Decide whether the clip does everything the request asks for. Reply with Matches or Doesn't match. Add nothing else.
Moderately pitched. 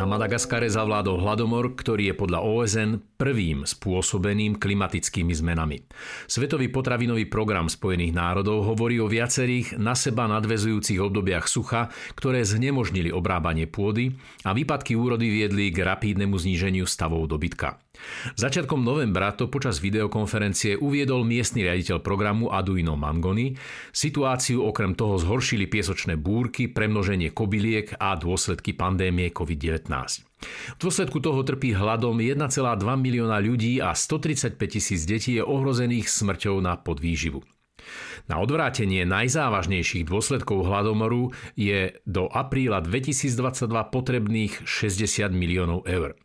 Doesn't match